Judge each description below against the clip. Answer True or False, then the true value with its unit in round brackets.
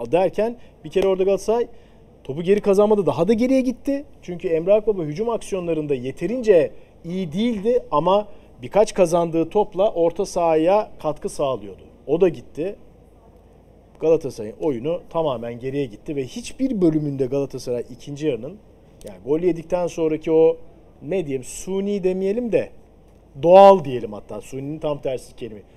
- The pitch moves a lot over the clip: True (5.8 semitones)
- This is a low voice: False (175 Hz)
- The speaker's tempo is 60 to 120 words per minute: False (135 wpm)